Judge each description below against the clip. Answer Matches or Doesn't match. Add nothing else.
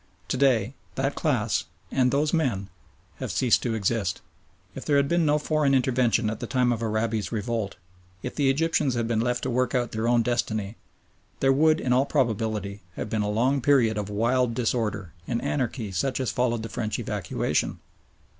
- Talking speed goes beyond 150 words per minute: Matches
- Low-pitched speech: Matches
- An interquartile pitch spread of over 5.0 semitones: Doesn't match